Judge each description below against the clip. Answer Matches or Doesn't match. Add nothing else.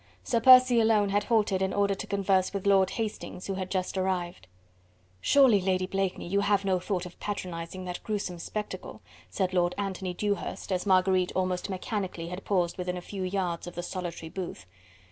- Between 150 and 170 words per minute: Doesn't match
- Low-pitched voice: Doesn't match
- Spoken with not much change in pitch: Matches